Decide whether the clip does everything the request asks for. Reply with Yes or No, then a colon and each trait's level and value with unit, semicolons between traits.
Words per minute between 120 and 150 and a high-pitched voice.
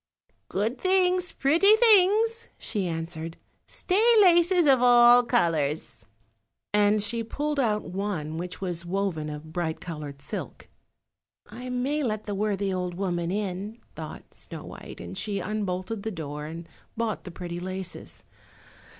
Yes: average, 140 wpm; high, 205 Hz